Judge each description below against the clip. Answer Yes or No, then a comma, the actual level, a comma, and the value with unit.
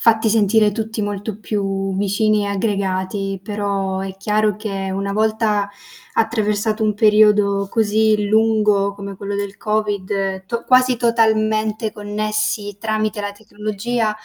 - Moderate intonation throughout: No, narrow, 1.5 semitones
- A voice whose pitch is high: Yes, high, 210 Hz